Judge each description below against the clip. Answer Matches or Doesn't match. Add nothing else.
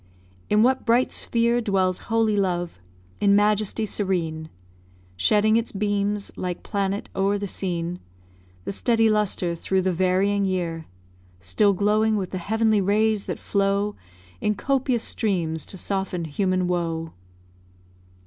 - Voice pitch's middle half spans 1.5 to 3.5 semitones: Matches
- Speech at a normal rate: Doesn't match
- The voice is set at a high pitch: Matches